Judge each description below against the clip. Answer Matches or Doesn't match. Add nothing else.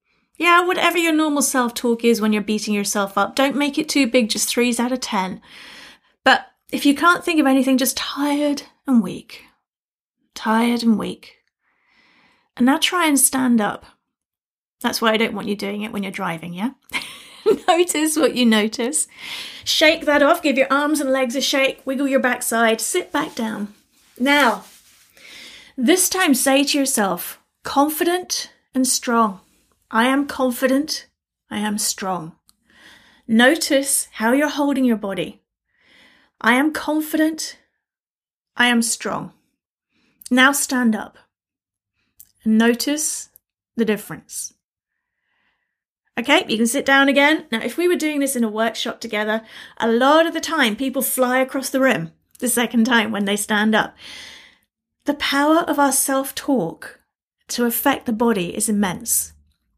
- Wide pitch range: Doesn't match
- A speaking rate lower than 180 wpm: Matches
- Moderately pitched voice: Doesn't match